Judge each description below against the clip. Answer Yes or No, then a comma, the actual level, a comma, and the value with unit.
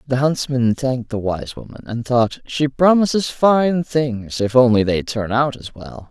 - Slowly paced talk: No, average, 185 wpm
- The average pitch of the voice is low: Yes, low, 130 Hz